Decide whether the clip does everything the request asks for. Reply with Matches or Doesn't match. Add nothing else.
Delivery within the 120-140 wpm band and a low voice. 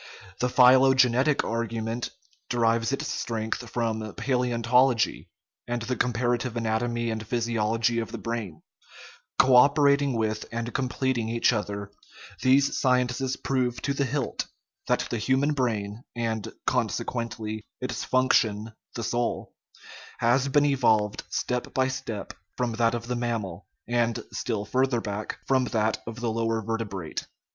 Matches